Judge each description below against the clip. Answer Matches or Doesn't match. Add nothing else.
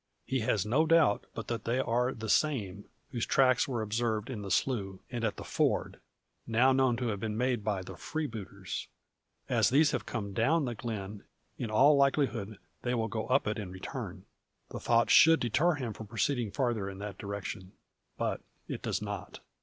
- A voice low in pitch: Matches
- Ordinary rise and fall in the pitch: Matches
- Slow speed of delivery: Doesn't match